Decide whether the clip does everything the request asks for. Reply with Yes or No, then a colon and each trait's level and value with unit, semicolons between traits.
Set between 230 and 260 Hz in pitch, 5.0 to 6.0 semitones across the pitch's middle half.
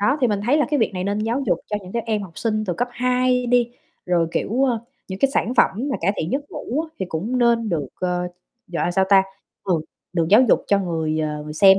No: high, 210 Hz; wide, 5.6 semitones